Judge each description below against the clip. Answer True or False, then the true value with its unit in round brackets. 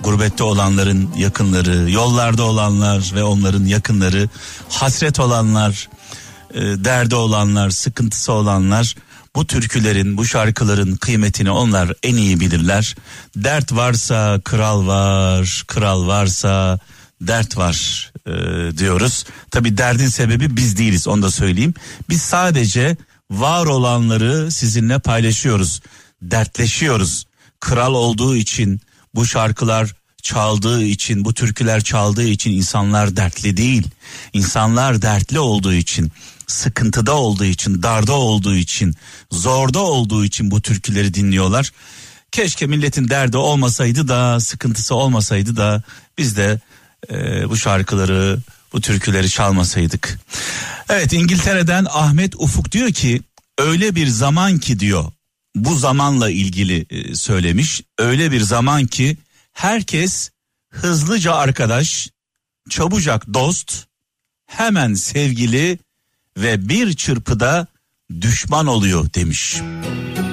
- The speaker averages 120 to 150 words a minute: False (110 wpm)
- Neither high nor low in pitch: False (115 Hz)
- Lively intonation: False (4.6 semitones)